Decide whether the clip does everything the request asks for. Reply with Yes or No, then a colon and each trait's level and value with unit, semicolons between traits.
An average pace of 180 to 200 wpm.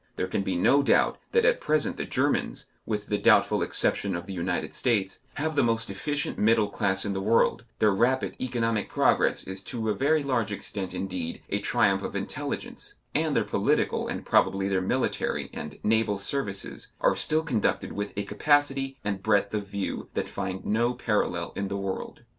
Yes: average, 185 wpm